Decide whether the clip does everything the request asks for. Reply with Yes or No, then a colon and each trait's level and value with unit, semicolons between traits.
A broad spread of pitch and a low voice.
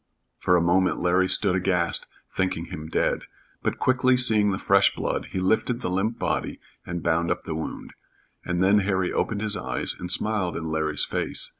No: average, 3.3 semitones; very low, 95 Hz